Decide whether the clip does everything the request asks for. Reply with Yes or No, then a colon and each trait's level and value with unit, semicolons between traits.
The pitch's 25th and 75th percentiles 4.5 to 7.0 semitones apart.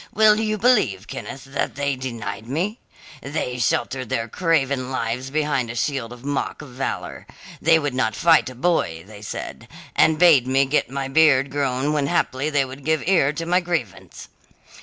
No: average, 3.9 semitones